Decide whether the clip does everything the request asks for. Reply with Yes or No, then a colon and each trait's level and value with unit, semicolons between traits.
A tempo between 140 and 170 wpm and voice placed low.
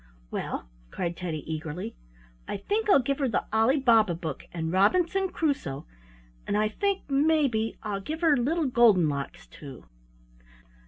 No: average, 150 wpm; high, 220 Hz